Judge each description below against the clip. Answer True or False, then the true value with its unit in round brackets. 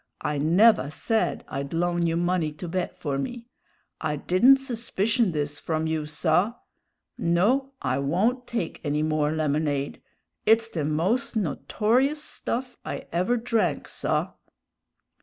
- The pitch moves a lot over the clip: True (7.0 semitones)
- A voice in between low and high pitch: True (175 Hz)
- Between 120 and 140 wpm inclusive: True (135 wpm)